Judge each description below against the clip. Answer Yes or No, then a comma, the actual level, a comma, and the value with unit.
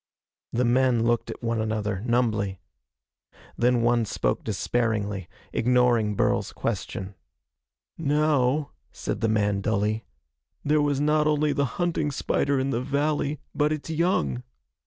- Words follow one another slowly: Yes, slow, 130 wpm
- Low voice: Yes, low, 125 Hz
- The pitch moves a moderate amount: Yes, average, 5.0 semitones